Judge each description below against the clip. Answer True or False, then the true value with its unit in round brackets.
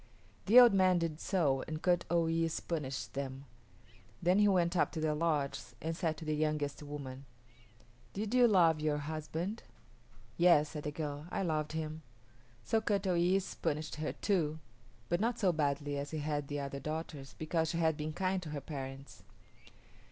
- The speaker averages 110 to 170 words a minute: False (180 wpm)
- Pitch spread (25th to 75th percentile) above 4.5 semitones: False (3.0 semitones)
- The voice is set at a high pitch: False (155 Hz)